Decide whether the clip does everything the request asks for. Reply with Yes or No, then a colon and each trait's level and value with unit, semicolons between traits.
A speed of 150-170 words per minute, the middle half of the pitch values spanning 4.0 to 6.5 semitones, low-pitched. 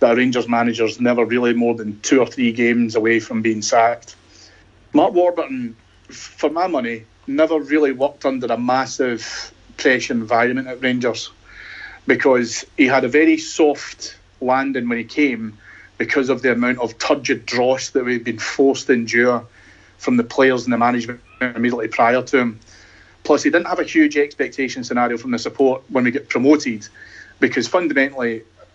No: average, 165 wpm; average, 2.7 semitones; low, 120 Hz